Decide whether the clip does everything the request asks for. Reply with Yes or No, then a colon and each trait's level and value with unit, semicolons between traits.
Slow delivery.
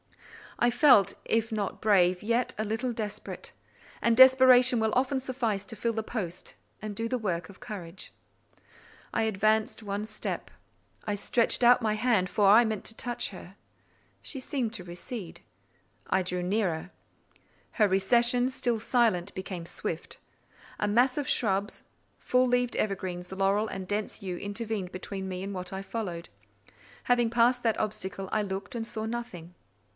No: average, 160 wpm